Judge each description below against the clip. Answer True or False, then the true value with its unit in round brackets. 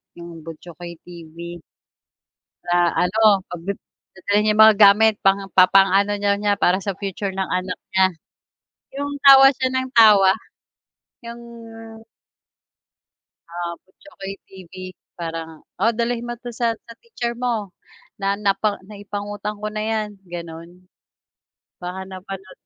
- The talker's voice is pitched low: False (195 Hz)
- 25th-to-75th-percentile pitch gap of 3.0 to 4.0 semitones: True (3.5 semitones)